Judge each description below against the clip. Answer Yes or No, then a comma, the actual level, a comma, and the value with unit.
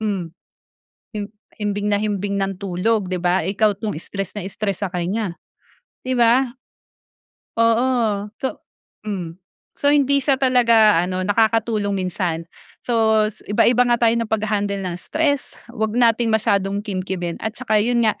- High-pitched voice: Yes, high, 210 Hz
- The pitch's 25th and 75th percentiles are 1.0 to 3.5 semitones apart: Yes, average, 2.9 semitones